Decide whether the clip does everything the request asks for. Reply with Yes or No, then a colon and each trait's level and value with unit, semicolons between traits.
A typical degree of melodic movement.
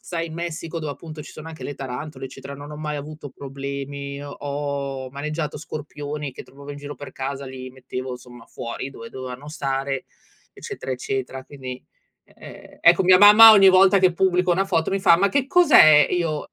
Yes: average, 3.5 semitones